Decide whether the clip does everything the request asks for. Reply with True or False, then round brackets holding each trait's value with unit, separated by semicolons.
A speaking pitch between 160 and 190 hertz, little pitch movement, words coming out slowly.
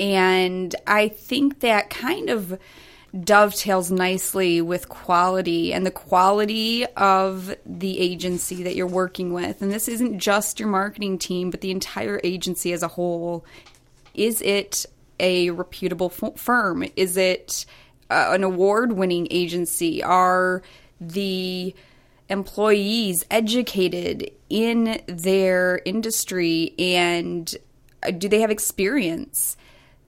True (185 Hz; 2.3 semitones; 115 wpm)